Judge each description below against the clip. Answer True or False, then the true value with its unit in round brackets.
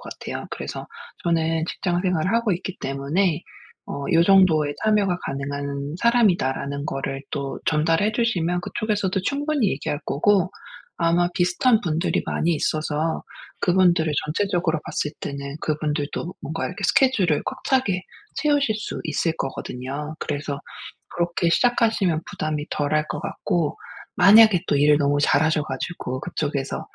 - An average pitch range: True (4.7 semitones)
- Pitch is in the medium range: True (165 Hz)